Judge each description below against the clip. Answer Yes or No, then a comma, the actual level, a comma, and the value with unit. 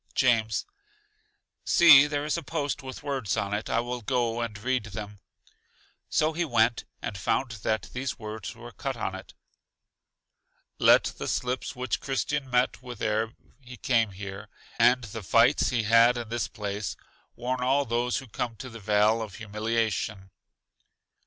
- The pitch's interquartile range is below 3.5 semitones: Yes, average, 3.0 semitones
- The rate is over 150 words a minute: Yes, average, 160 wpm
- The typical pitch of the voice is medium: No, low, 115 Hz